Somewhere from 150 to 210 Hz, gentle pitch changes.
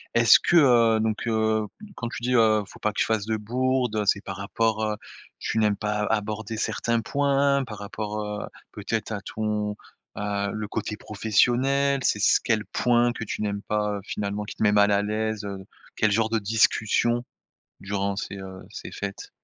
No: low, 110 Hz; narrow, 1.9 semitones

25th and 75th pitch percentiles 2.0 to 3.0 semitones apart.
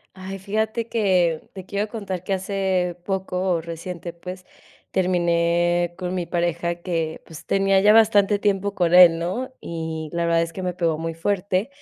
Yes: narrow, 2.5 semitones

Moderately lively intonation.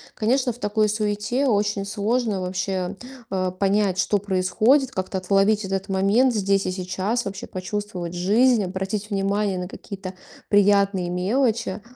No: narrow, 2.1 semitones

